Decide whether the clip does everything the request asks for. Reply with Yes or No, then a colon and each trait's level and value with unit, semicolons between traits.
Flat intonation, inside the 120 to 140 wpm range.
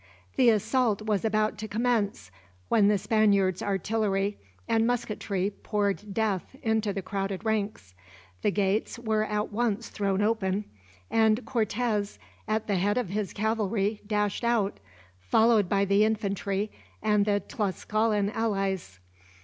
Yes: narrow, 1.8 semitones; slow, 135 wpm